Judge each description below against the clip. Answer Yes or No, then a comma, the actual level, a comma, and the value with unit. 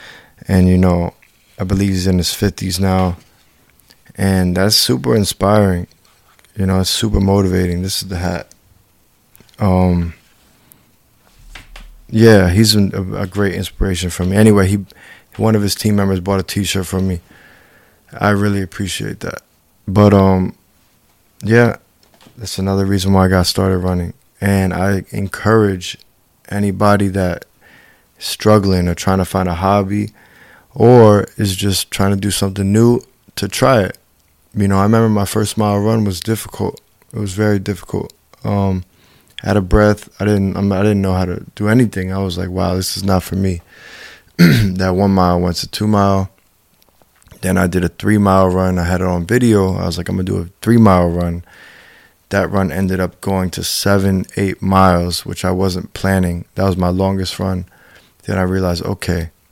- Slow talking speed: No, average, 170 wpm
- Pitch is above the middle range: No, very low, 95 Hz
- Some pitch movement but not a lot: No, narrow, 1.9 semitones